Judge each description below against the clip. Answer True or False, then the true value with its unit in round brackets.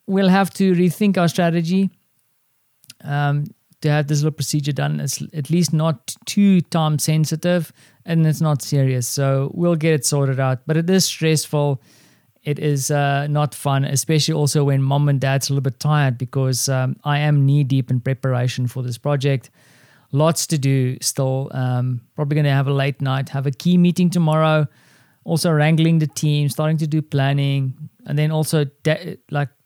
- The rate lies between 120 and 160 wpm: False (180 wpm)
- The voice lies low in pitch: False (145 Hz)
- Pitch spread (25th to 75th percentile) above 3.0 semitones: False (2.7 semitones)